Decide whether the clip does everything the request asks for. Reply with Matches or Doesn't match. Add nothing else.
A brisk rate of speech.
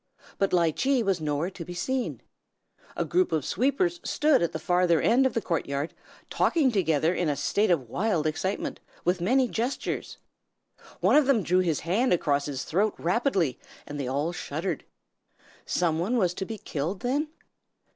Doesn't match